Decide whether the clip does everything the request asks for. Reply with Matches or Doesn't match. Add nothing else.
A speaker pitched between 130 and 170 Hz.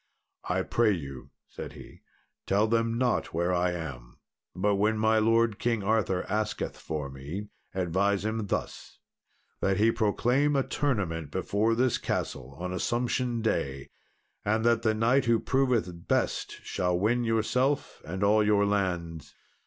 Doesn't match